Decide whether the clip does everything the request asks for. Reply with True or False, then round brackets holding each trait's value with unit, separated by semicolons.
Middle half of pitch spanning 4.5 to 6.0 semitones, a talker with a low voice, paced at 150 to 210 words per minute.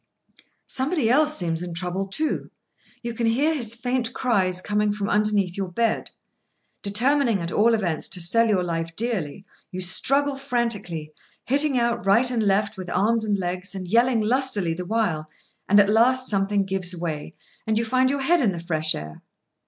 False (4.9 semitones; 210 Hz; 175 wpm)